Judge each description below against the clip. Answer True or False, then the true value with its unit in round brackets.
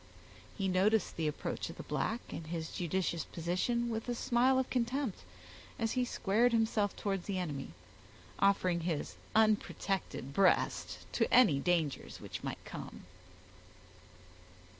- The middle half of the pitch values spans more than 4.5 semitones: True (5.2 semitones)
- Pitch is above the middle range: True (195 Hz)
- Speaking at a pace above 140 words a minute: False (135 wpm)